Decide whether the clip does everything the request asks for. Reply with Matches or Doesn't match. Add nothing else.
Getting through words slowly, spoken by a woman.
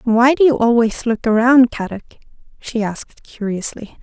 Doesn't match